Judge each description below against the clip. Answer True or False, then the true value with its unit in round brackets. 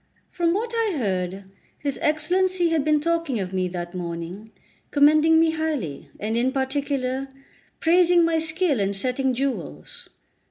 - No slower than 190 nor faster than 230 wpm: False (145 wpm)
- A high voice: True (280 Hz)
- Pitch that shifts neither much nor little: False (8.4 semitones)